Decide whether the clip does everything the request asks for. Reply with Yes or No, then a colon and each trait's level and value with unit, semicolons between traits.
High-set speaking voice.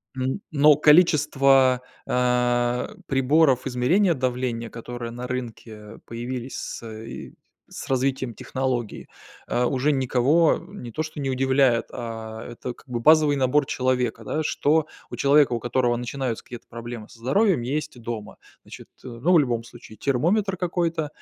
No: low, 130 Hz